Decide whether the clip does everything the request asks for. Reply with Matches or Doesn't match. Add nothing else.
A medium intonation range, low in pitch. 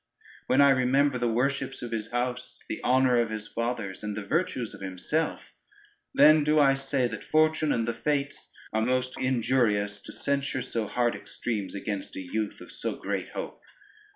Matches